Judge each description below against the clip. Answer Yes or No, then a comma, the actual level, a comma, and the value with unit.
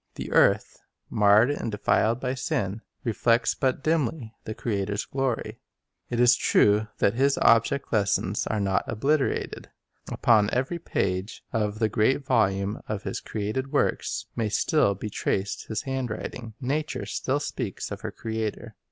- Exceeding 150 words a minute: No, average, 145 wpm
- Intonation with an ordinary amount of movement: Yes, average, 4.1 semitones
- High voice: No, low, 115 Hz